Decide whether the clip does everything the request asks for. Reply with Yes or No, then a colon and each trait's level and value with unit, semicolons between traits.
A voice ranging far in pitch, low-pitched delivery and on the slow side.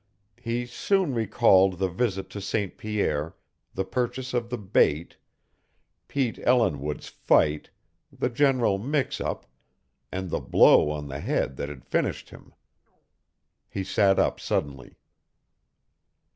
Yes: wide, 7.1 semitones; low, 100 Hz; slow, 125 wpm